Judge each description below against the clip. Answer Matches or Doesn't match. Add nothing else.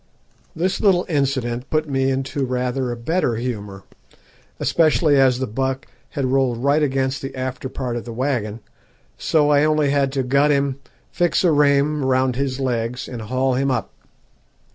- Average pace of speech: Matches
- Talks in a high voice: Doesn't match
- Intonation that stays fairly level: Matches